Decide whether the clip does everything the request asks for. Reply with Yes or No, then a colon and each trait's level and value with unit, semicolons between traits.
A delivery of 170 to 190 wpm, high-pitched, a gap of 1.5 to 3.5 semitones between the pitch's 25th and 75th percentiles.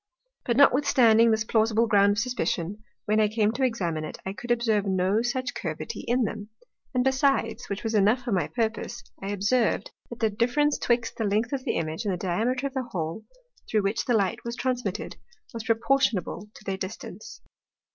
Yes: average, 185 wpm; high, 220 Hz; average, 3.2 semitones